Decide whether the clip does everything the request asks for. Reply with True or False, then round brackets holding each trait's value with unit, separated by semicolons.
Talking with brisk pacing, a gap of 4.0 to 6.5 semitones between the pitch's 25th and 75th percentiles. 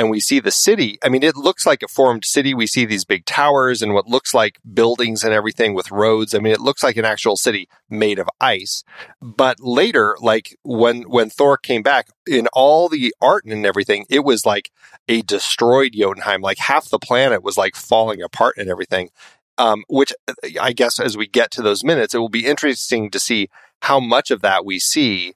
True (215 wpm; 4.4 semitones)